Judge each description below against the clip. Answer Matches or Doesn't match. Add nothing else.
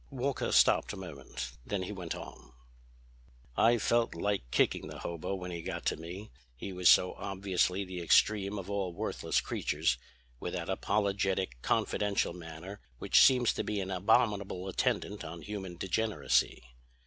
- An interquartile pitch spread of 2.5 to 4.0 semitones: Matches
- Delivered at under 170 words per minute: Matches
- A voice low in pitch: Matches